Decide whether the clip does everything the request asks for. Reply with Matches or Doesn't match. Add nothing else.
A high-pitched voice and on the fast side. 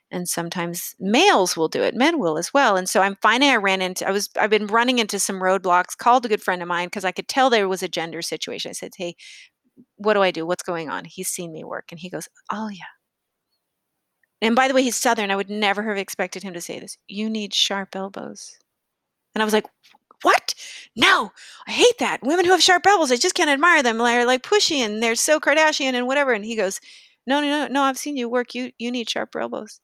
Matches